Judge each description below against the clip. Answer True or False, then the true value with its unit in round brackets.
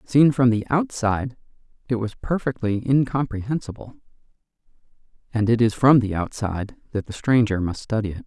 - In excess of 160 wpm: False (145 wpm)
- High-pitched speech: False (115 Hz)